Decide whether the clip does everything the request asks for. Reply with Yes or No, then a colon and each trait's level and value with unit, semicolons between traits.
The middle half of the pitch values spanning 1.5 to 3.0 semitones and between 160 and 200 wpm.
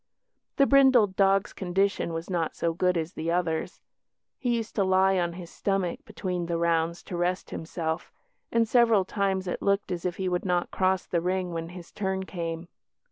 Yes: narrow, 2.4 semitones; average, 190 wpm